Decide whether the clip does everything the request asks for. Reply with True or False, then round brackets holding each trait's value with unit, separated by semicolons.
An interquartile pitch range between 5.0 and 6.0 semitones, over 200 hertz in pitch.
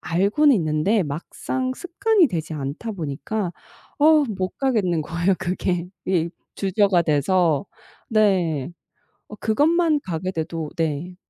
False (5.3 semitones; 185 Hz)